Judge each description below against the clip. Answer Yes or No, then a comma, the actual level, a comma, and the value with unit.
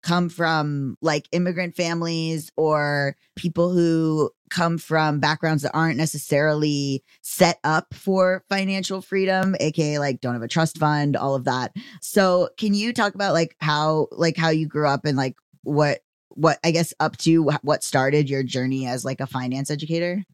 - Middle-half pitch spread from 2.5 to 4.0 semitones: Yes, average, 2.9 semitones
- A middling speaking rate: Yes, average, 170 wpm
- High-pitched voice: No, medium, 155 Hz